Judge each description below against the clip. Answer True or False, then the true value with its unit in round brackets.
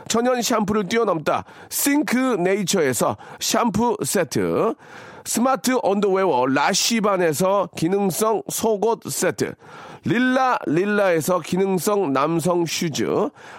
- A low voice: False (210 Hz)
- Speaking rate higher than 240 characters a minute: False (230 characters per minute)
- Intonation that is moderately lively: True (3.9 semitones)